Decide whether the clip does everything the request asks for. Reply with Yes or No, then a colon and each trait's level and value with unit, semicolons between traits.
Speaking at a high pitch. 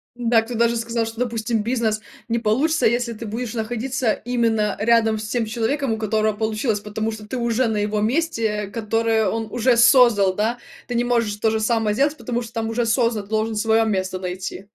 Yes: high, 225 Hz